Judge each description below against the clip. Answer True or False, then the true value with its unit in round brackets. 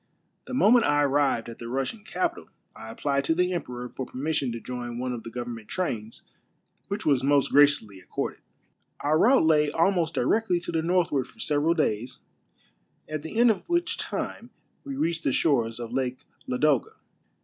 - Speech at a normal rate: True (175 wpm)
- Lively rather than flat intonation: True (5.7 semitones)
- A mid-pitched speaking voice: True (145 Hz)